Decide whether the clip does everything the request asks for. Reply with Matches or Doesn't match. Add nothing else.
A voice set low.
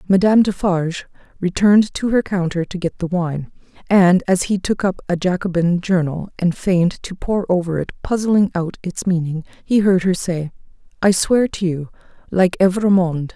Doesn't match